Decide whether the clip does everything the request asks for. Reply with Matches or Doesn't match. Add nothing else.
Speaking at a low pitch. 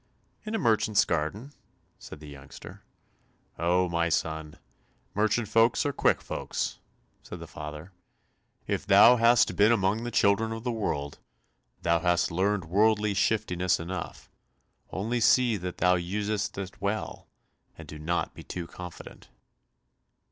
Matches